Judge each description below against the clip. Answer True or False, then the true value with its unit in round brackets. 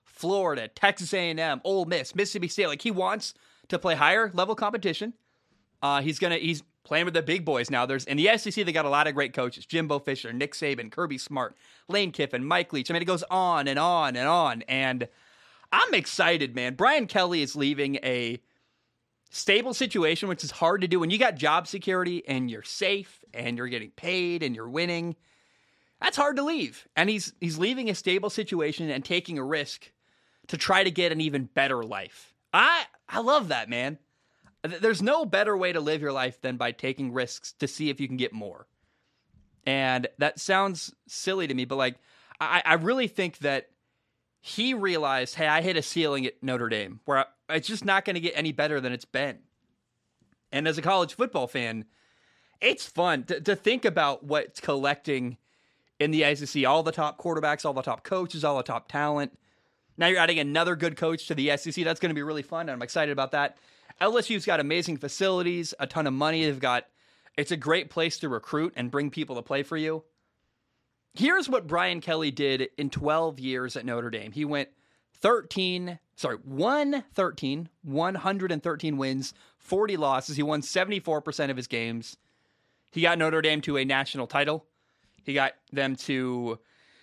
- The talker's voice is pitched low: False (155 Hz)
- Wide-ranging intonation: False (4.9 semitones)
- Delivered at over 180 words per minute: True (190 wpm)